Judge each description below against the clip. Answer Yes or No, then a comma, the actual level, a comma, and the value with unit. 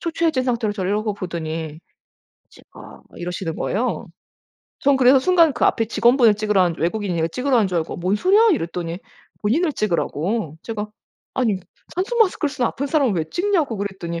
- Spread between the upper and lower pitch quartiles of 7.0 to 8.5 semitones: Yes, wide, 7.5 semitones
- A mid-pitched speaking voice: No, high, 215 Hz